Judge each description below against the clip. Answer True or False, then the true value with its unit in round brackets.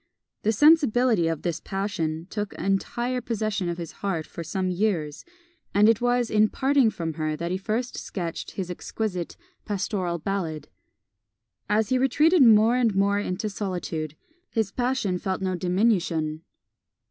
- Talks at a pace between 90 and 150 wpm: True (145 wpm)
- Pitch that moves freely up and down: False (4.7 semitones)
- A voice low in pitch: False (195 Hz)